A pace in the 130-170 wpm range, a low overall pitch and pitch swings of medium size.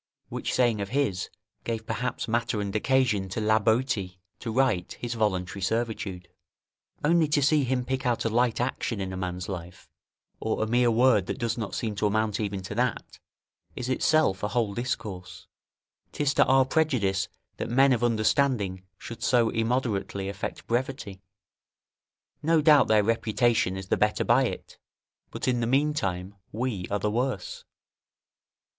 Yes: average, 165 wpm; low, 115 Hz; average, 4.1 semitones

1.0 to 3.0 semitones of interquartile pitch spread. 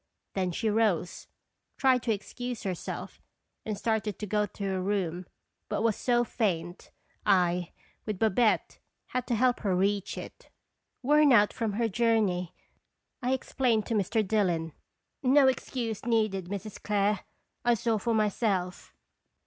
No: average, 3.5 semitones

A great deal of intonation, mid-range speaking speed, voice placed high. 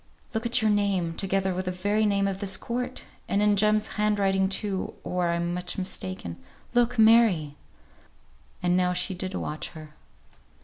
No: average, 2.8 semitones; average, 170 wpm; high, 195 Hz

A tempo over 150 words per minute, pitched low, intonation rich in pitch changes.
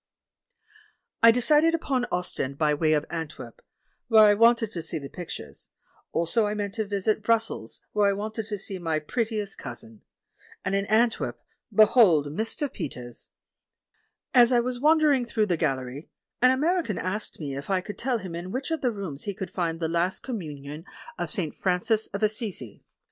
No: average, 185 wpm; high, 205 Hz; wide, 6.0 semitones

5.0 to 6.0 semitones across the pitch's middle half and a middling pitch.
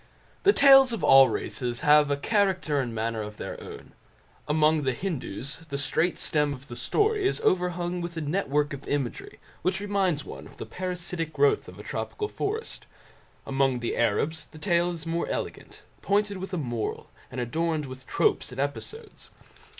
Yes: wide, 5.6 semitones; medium, 160 Hz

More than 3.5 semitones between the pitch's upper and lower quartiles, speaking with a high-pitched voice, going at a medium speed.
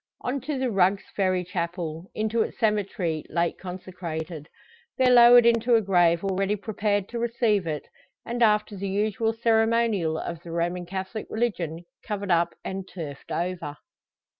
Yes: average, 4.4 semitones; high, 195 Hz; average, 150 wpm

